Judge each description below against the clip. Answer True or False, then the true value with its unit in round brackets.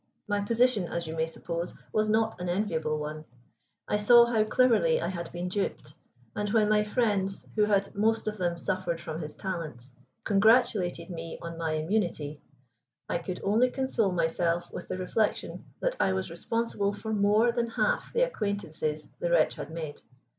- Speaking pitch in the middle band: False (195 Hz)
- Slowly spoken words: False (175 wpm)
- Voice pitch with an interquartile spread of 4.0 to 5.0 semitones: True (4.6 semitones)